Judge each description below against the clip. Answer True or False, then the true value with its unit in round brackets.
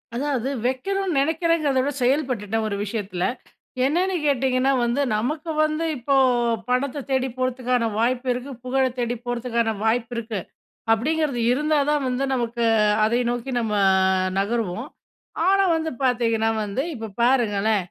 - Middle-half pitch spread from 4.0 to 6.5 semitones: False (3.5 semitones)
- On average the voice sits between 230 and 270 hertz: True (250 Hz)